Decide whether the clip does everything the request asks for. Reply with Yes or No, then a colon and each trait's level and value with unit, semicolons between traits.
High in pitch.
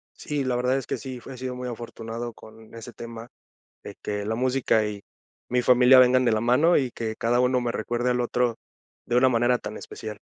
No: low, 120 Hz